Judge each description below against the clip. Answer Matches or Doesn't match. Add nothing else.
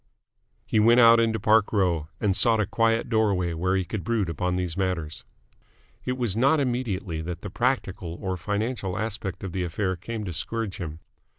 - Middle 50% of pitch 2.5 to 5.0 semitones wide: Matches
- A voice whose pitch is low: Matches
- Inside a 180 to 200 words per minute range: Matches